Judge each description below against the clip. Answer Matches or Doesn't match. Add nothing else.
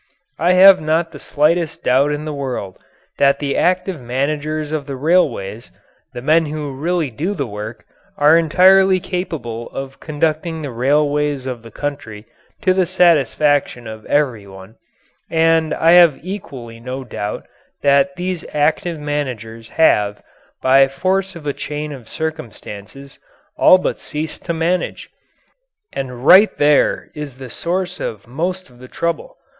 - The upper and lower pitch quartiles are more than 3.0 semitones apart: Matches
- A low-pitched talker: Doesn't match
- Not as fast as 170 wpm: Matches